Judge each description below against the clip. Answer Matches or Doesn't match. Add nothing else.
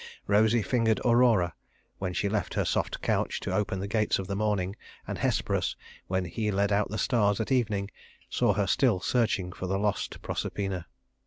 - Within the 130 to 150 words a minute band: Doesn't match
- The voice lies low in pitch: Matches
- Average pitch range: Doesn't match